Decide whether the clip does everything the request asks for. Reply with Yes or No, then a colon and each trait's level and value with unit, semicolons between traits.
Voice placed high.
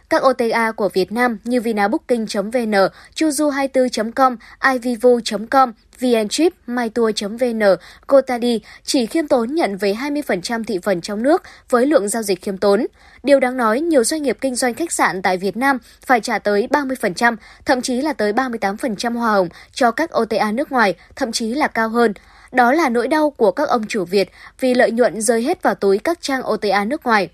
Yes: high, 240 Hz